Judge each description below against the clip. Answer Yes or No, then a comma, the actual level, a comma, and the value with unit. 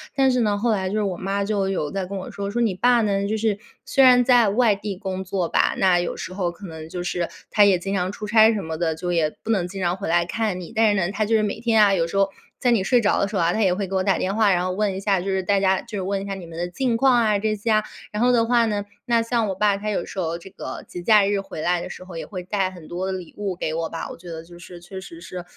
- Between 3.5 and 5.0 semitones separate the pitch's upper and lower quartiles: No, average, 3.0 semitones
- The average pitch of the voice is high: Yes, high, 195 Hz